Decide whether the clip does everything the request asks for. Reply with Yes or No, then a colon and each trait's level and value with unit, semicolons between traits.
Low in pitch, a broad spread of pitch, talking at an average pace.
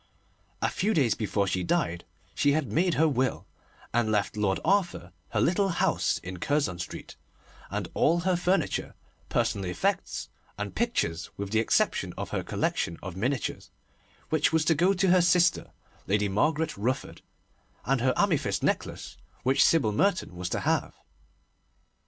Yes: low, 130 Hz; wide, 9.0 semitones; average, 155 wpm